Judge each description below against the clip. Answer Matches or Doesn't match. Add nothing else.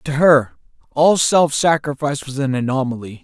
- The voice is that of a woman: Doesn't match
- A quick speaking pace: Doesn't match